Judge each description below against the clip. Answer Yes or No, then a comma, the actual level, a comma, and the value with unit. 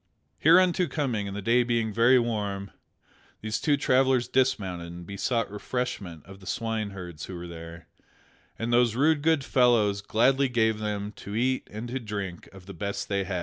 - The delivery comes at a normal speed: Yes, average, 175 wpm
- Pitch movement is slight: No, average, 4.1 semitones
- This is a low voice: Yes, low, 110 Hz